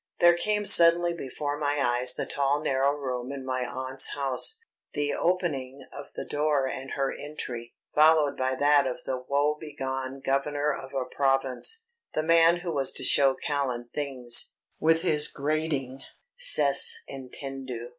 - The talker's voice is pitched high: No, medium, 140 Hz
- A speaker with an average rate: Yes, average, 150 wpm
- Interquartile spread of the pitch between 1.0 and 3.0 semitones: Yes, narrow, 2.5 semitones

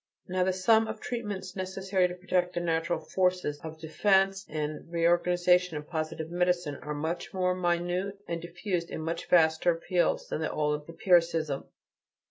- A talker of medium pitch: Yes, medium, 175 Hz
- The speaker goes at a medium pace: Yes, average, 160 wpm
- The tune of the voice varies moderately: No, narrow, 2.3 semitones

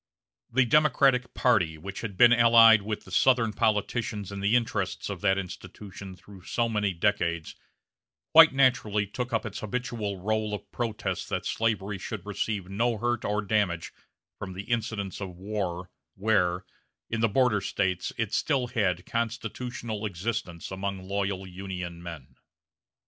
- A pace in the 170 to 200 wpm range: No, average, 150 wpm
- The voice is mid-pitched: No, low, 105 Hz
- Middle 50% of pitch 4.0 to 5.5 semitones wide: No, average, 3.4 semitones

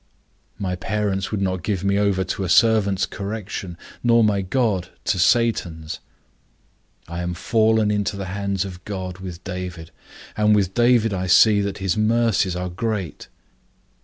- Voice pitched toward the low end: Yes, low, 100 Hz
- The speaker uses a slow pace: No, average, 155 wpm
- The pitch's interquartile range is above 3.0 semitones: No, average, 2.7 semitones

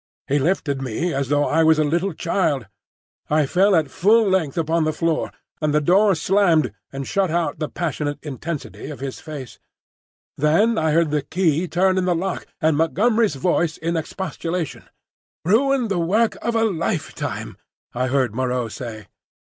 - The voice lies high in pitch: No, medium, 160 Hz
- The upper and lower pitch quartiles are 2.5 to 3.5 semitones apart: No, average, 4.4 semitones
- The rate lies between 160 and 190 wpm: Yes, average, 170 wpm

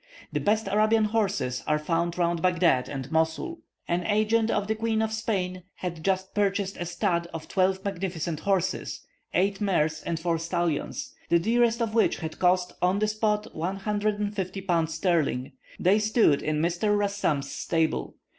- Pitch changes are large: No, average, 4.0 semitones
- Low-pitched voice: No, medium, 185 Hz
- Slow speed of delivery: No, average, 160 wpm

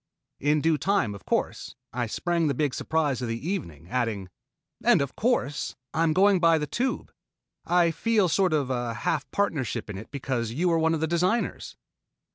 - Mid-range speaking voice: Yes, medium, 155 Hz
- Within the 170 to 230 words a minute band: Yes, average, 185 wpm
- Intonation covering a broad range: Yes, wide, 5.8 semitones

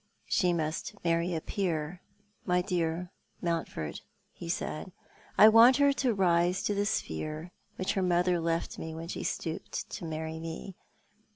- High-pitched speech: No, medium, 175 Hz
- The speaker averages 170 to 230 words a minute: No, average, 150 wpm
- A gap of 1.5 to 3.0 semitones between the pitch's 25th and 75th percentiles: Yes, narrow, 2.4 semitones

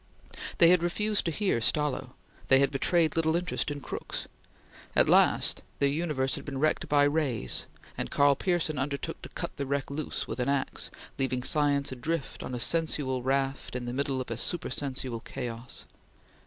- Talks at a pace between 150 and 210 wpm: Yes, average, 175 wpm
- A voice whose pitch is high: No, medium, 140 Hz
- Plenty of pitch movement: No, average, 3.1 semitones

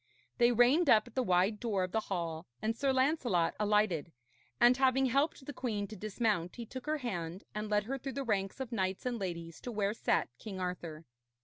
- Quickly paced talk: Yes, fast, 210 wpm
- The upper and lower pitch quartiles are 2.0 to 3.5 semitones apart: No, average, 5.2 semitones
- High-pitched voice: Yes, high, 215 Hz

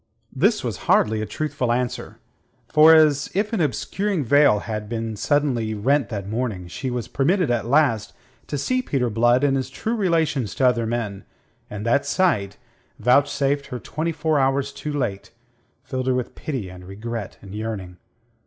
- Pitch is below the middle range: Yes, low, 130 Hz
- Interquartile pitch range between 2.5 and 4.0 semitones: No, average, 5.0 semitones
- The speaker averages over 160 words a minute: Yes, average, 170 wpm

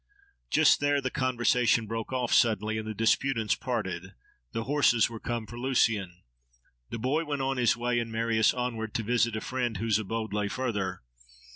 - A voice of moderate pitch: No, low, 115 Hz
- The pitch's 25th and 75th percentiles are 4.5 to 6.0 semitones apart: No, narrow, 2.5 semitones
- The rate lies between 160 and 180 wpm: Yes, average, 175 wpm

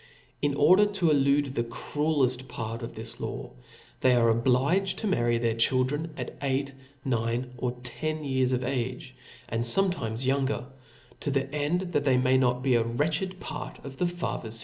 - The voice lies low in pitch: Yes, low, 130 Hz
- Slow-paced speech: No, average, 175 wpm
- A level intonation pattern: No, average, 3.4 semitones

